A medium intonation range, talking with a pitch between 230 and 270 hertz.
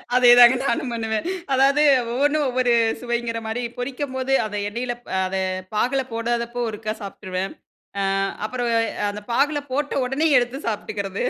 Yes: average, 3.0 semitones; high, 240 Hz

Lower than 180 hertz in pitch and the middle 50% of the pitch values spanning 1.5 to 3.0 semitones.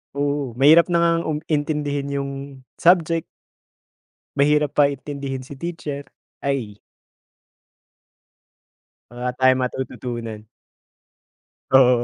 Yes: medium, 140 Hz; narrow, 2.4 semitones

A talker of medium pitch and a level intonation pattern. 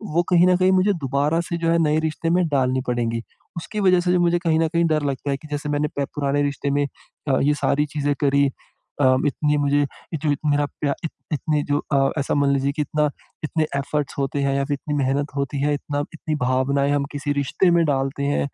Yes: medium, 145 Hz; narrow, 2.1 semitones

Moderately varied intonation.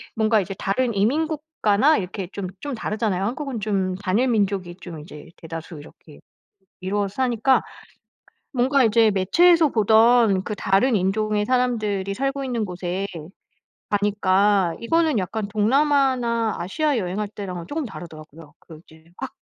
Yes: average, 4.7 semitones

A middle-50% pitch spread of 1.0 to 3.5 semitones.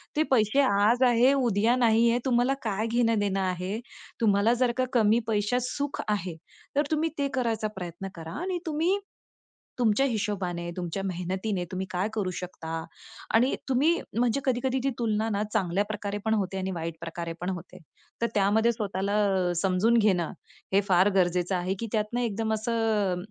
No: average, 4.1 semitones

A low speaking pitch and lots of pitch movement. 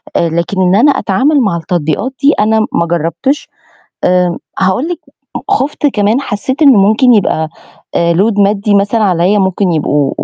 No: high, 200 Hz; wide, 6.1 semitones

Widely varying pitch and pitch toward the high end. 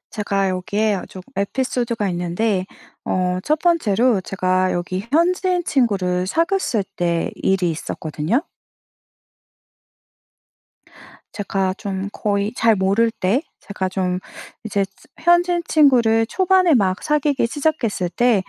Yes: wide, 6.2 semitones; high, 210 Hz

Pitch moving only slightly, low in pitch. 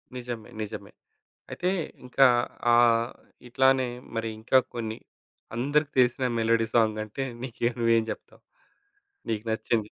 Yes: narrow, 2.3 semitones; low, 115 Hz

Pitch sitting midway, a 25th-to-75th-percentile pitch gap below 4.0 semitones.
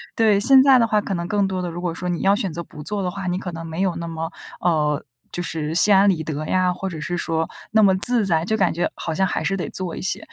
Yes: medium, 180 Hz; average, 3.2 semitones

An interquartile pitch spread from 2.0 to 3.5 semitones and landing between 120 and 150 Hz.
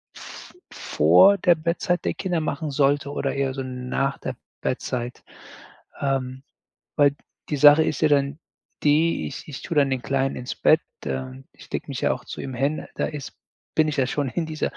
Yes: average, 2.7 semitones; medium, 140 Hz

